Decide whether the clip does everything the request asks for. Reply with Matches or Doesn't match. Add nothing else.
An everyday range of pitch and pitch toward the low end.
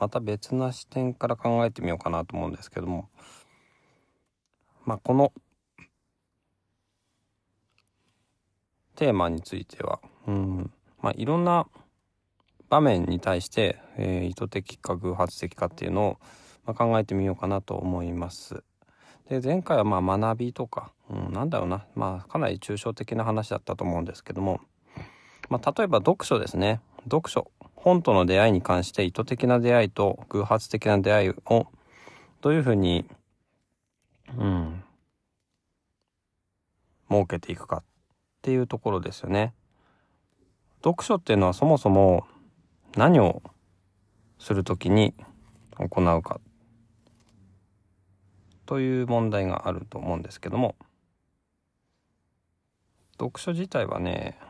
Matches